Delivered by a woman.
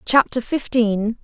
Yes: female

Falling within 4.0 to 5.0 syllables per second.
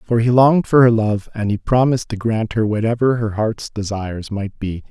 No: 5.5 syllables/s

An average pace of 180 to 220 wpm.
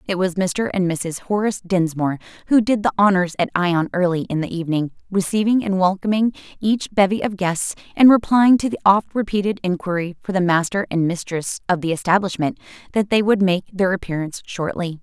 Yes: average, 185 wpm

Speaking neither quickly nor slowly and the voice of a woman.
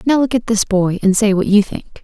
No: fast, 295 wpm; female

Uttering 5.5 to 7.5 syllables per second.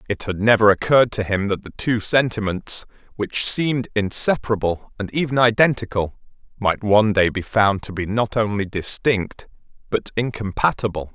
No: 5.1 syllables/s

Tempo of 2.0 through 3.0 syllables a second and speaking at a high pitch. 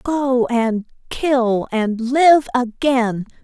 Yes: 2.4 syllables/s; high, 245 Hz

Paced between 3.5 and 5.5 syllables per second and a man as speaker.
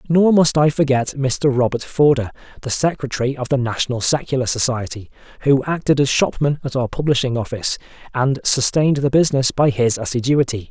No: 5.7 syllables/s; male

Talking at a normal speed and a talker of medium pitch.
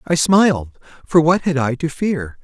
Yes: average, 175 wpm; medium, 150 Hz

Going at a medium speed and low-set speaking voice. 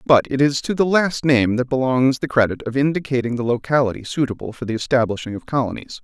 No: fast, 210 wpm; low, 130 Hz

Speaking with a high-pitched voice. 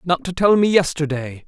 No: medium, 165 Hz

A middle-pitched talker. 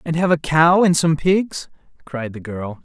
Yes: medium, 155 Hz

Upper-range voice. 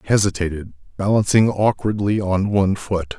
No: low, 100 Hz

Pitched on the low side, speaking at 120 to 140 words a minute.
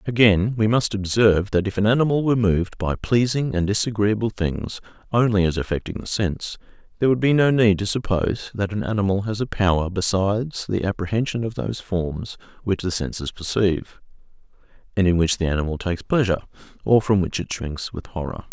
No: low, 100 Hz; average, 185 wpm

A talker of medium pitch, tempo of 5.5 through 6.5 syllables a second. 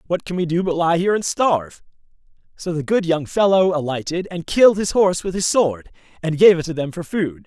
Yes: medium, 170 Hz; 5.8 syllables/s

